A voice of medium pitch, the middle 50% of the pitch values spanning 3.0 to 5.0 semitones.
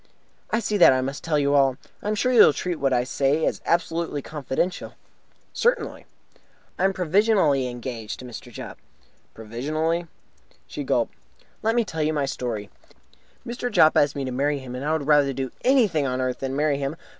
Yes: medium, 145 Hz; average, 4.6 semitones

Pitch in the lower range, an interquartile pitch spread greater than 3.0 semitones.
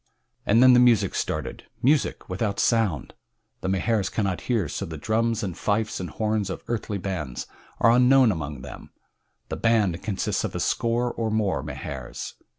Yes: low, 105 Hz; average, 4.0 semitones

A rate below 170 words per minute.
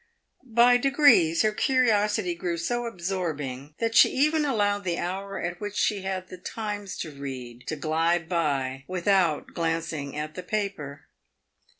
Yes: average, 155 wpm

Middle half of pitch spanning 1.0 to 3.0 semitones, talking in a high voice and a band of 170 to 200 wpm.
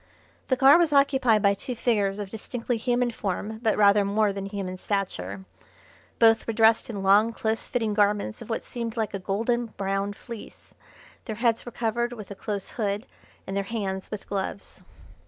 Yes: average, 2.7 semitones; high, 215 Hz; average, 180 wpm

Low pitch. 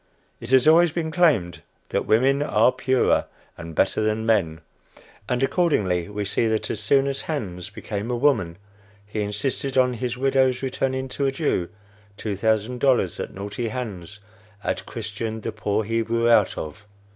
Yes: low, 115 Hz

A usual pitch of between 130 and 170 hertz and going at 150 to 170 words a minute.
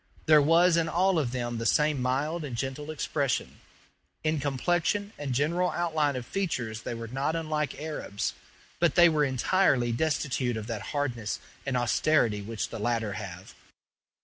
Yes: medium, 140 Hz; average, 160 wpm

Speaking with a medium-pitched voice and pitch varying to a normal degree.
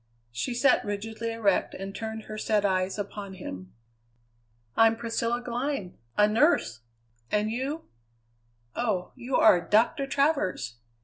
No: high, 220 Hz; average, 3.5 semitones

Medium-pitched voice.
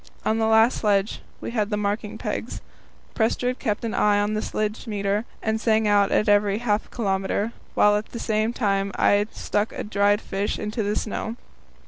No: high, 210 Hz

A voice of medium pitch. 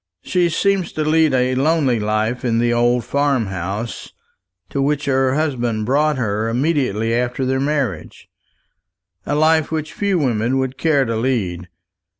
No: low, 130 Hz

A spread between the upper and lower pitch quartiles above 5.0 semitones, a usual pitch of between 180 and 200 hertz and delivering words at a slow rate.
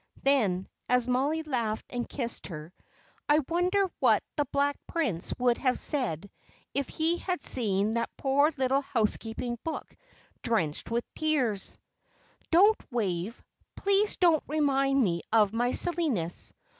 No: wide, 5.5 semitones; very high, 255 Hz; slow, 130 wpm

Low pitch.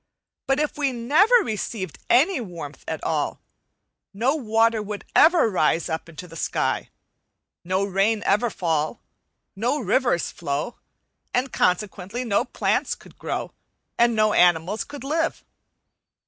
No: high, 215 Hz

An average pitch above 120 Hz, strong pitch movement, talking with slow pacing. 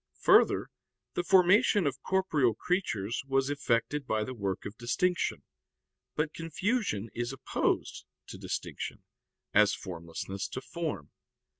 Yes: low, 135 Hz; wide, 8.5 semitones; slow, 120 wpm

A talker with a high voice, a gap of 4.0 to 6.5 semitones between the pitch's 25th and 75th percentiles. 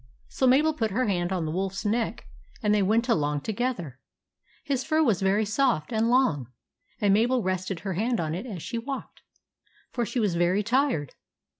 Yes: high, 210 Hz; average, 5.1 semitones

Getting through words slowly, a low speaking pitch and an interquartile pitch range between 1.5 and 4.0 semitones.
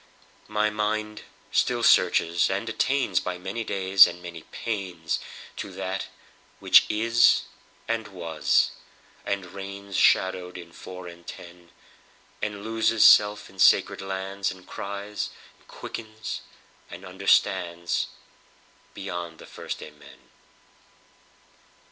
Yes: slow, 95 wpm; very low, 95 Hz; average, 3.1 semitones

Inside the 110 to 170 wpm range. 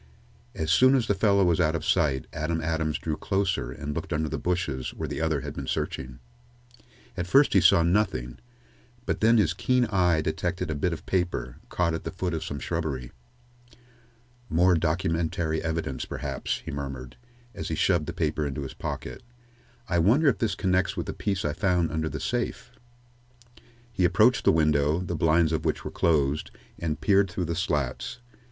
No: average, 185 wpm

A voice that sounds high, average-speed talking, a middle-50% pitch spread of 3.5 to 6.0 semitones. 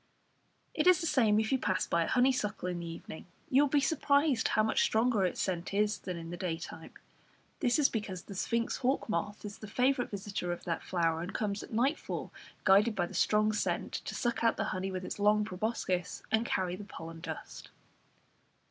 No: high, 210 Hz; fast, 210 wpm; average, 4.7 semitones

